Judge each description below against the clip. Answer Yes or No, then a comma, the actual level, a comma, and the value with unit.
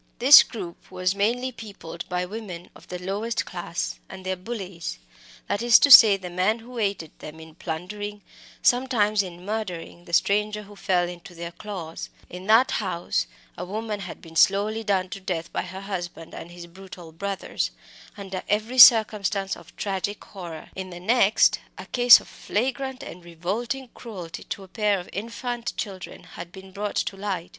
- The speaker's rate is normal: Yes, average, 180 wpm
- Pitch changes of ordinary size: Yes, average, 3.3 semitones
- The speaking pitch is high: Yes, high, 195 Hz